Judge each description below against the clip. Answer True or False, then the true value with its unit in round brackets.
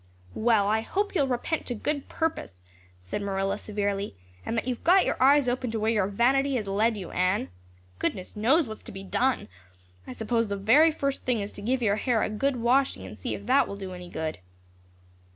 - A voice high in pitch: True (220 Hz)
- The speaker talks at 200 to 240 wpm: True (205 wpm)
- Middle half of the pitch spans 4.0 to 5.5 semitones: True (4.7 semitones)